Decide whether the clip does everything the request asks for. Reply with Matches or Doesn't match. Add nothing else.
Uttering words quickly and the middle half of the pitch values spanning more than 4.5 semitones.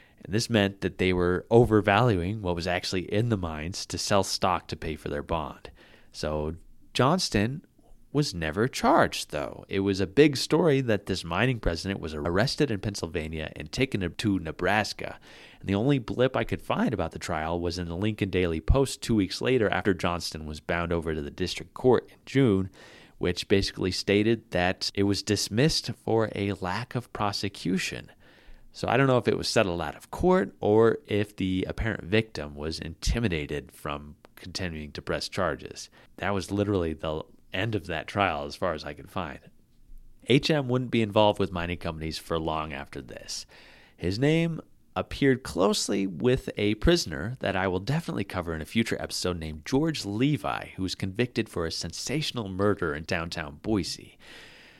Doesn't match